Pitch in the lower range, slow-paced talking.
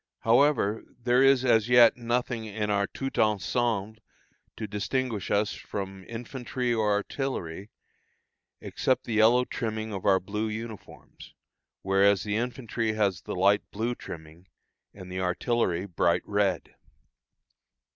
Yes: low, 110 Hz; slow, 125 wpm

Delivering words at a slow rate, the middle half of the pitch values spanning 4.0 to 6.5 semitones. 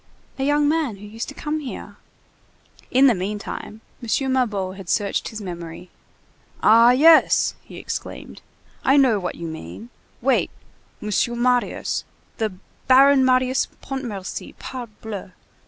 Yes: slow, 125 wpm; average, 4.6 semitones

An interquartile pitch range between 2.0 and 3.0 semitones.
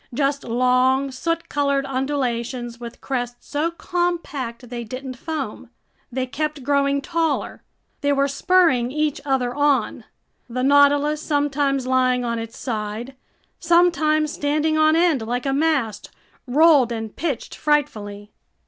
No: average, 3.5 semitones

